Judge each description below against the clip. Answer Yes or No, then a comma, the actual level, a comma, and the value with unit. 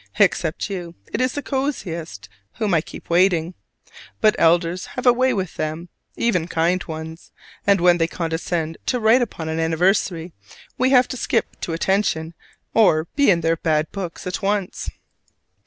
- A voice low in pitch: No, medium, 175 Hz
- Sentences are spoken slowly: No, average, 165 wpm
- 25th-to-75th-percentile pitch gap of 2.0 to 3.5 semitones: No, average, 4.3 semitones